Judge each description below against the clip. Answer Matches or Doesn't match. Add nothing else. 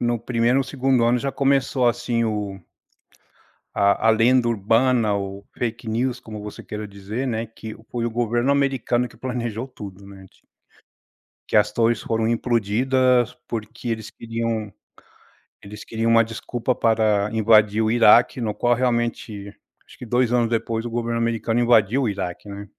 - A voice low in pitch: Matches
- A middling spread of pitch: Doesn't match